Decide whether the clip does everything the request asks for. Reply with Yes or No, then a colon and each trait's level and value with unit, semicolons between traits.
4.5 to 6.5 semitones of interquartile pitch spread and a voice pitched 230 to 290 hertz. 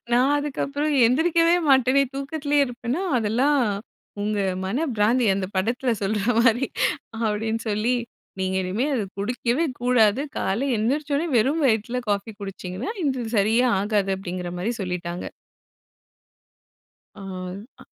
Yes: average, 4.8 semitones; high, 235 Hz